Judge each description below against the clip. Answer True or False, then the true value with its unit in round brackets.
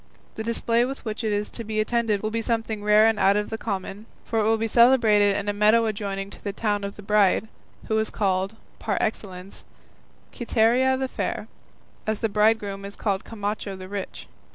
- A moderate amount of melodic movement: False (1.8 semitones)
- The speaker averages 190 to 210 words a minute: True (200 wpm)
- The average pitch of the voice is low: False (215 Hz)